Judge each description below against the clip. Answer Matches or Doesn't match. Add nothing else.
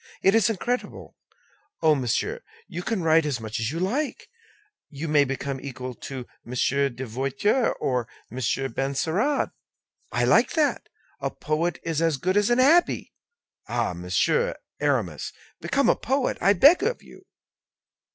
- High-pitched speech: Doesn't match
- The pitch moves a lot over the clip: Matches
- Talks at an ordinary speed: Matches